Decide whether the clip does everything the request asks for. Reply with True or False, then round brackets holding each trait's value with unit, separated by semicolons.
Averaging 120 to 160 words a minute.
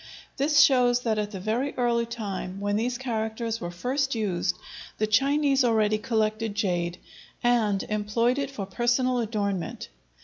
True (145 wpm)